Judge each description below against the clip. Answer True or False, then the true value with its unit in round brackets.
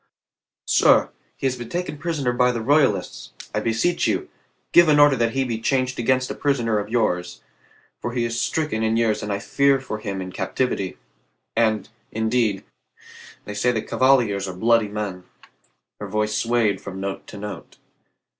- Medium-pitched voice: False (115 Hz)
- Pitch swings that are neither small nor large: True (3.8 semitones)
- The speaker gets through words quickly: False (175 wpm)